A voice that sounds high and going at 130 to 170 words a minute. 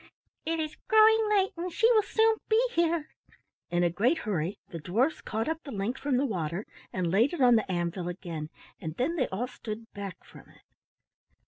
No: high, 245 Hz; average, 200 wpm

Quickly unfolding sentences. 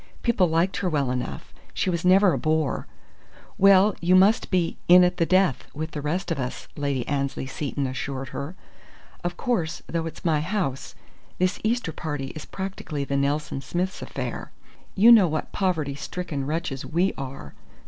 No: average, 170 wpm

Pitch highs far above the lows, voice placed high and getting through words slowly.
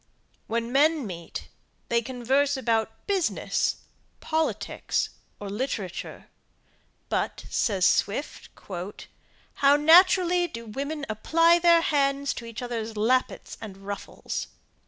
Yes: wide, 5.9 semitones; very high, 255 Hz; slow, 105 wpm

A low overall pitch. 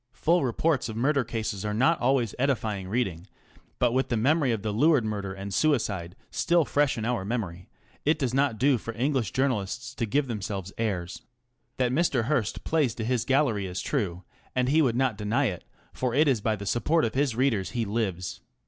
Yes: low, 120 Hz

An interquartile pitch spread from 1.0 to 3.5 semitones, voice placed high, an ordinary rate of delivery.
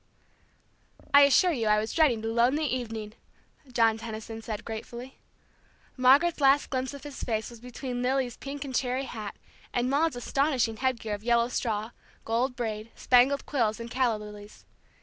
Yes: average, 3.1 semitones; high, 245 Hz; average, 160 wpm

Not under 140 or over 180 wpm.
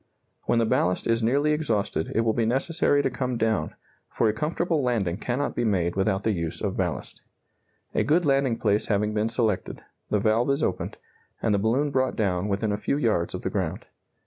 No: average, 200 wpm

